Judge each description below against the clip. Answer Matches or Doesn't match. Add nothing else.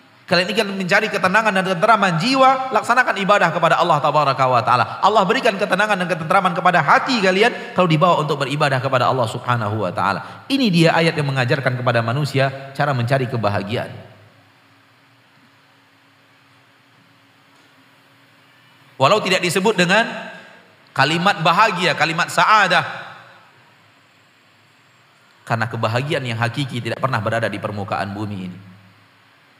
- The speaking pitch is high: Doesn't match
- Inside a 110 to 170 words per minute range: Matches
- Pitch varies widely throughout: Matches